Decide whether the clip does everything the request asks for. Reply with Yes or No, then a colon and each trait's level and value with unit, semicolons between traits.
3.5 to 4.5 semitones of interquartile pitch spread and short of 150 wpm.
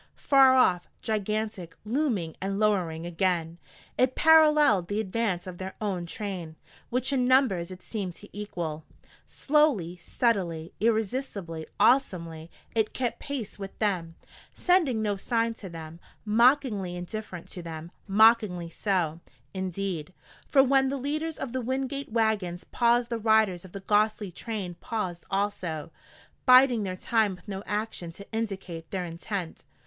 No: average, 4.9 semitones; average, 140 wpm